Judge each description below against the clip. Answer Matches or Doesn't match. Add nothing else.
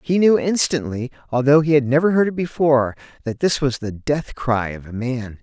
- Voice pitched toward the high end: Doesn't match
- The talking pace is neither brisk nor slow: Doesn't match